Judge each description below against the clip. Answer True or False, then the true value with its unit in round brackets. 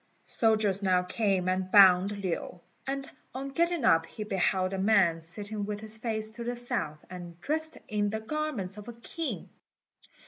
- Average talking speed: True (170 wpm)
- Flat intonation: False (4.1 semitones)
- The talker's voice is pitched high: True (210 Hz)